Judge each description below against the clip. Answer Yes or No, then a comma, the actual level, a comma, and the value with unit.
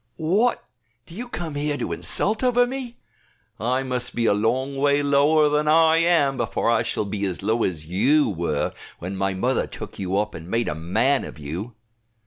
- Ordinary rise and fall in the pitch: No, wide, 7.5 semitones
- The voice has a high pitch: No, low, 130 Hz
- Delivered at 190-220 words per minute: Yes, average, 195 wpm